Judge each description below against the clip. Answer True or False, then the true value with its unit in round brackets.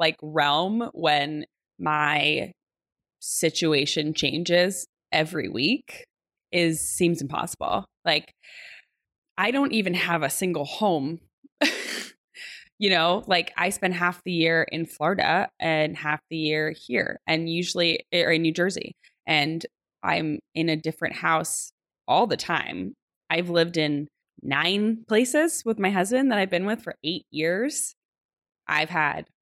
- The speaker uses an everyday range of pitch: True (3.7 semitones)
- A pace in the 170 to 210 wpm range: False (135 wpm)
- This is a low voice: False (170 Hz)